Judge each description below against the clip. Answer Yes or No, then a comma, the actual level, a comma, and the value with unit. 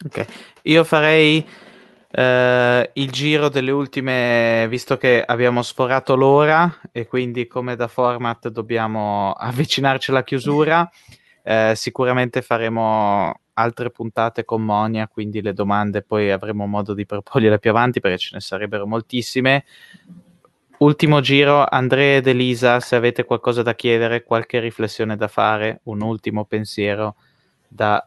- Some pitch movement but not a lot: Yes, average, 3.5 semitones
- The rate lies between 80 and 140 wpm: Yes, average, 135 wpm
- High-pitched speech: No, low, 120 Hz